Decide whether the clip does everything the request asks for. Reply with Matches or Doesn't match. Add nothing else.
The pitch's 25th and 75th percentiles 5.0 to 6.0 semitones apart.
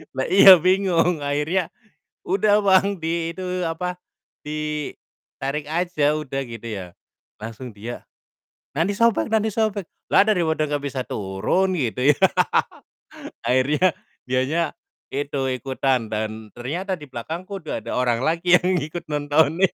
Matches